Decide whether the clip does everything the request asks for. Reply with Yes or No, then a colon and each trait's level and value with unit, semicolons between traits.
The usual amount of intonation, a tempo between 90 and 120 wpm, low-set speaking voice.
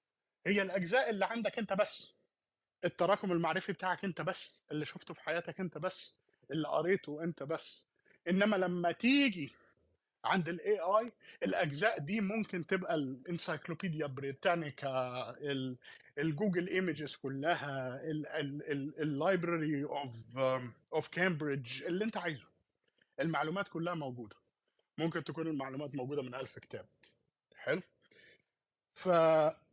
No: average, 4.5 semitones; average, 110 wpm; medium, 165 Hz